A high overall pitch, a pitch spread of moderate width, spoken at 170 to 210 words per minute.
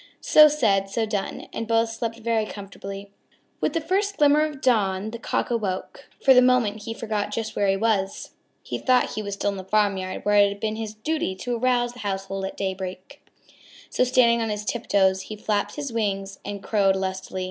Yes: high, 215 Hz; average, 3.4 semitones; average, 200 wpm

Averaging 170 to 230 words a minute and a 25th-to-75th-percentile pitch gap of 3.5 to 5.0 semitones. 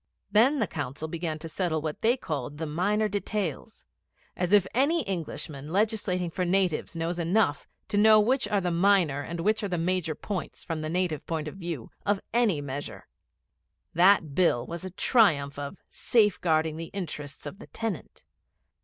Yes: average, 175 wpm; average, 4.6 semitones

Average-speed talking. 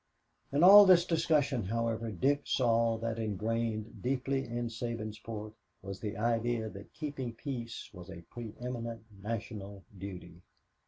No: slow, 125 wpm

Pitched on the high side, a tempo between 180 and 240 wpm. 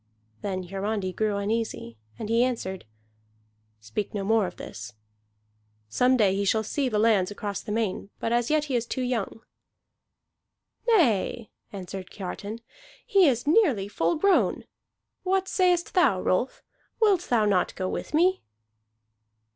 No: high, 220 Hz; average, 145 wpm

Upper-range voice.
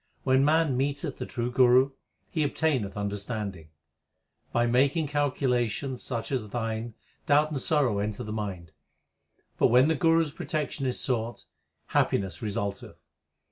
No: low, 125 Hz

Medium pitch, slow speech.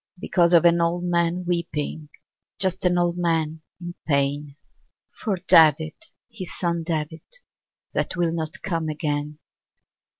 Yes: medium, 170 Hz; slow, 130 wpm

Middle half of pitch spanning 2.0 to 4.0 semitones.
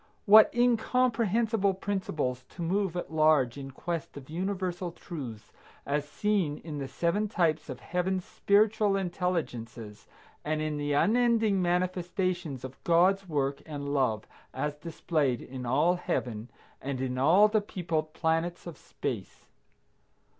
No: average, 5.3 semitones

